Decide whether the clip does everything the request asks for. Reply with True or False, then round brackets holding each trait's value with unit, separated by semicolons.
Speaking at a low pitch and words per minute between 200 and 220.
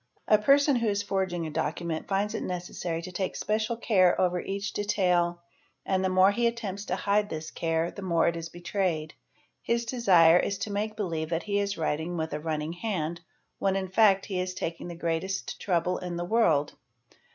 False (185 Hz; 205 wpm)